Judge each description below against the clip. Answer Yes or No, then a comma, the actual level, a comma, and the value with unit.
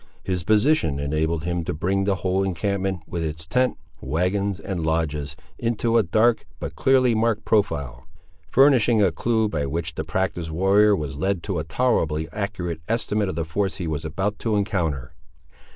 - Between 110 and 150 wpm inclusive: No, average, 170 wpm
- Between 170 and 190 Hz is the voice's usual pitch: No, very low, 95 Hz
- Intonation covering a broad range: No, average, 4.8 semitones